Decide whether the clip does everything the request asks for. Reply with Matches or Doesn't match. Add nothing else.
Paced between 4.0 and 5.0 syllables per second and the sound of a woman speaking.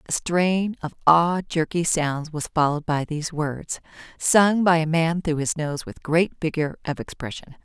Matches